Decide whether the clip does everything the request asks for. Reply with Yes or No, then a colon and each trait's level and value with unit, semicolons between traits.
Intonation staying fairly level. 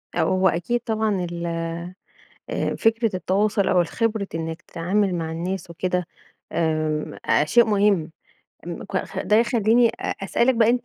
No: average, 4.7 semitones